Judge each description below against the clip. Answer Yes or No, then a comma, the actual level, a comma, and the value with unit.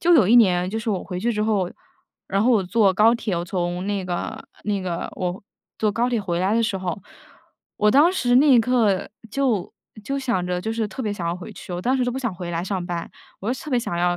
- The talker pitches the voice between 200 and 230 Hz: Yes, high, 205 Hz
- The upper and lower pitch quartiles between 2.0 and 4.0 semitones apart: No, average, 4.8 semitones